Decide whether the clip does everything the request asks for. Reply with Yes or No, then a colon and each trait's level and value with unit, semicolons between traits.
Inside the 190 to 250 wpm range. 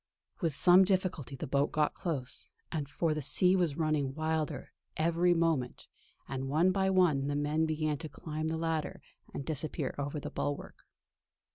No: average, 160 wpm